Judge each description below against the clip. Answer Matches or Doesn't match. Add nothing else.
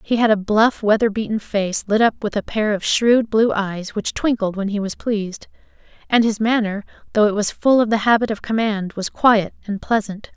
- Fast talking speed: Matches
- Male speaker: Doesn't match